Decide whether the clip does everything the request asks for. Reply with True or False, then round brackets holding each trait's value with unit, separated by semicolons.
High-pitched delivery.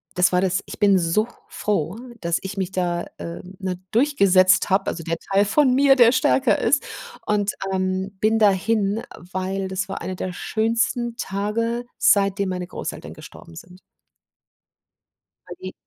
True (195 Hz)